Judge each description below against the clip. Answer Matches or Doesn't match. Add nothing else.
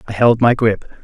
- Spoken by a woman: Doesn't match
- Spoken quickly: Matches